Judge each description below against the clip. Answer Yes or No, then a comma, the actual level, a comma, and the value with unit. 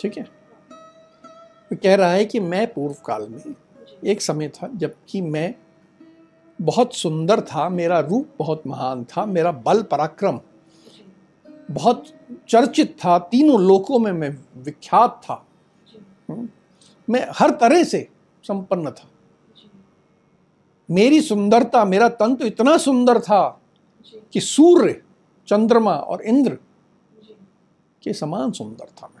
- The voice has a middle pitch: No, high, 210 Hz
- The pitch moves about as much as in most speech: No, wide, 6.0 semitones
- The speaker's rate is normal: Yes, average, 125 wpm